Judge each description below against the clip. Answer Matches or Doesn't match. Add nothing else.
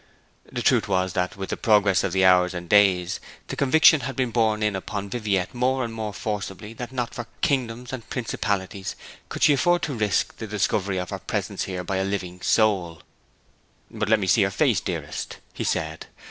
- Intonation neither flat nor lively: Matches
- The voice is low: Matches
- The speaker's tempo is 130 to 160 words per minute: Doesn't match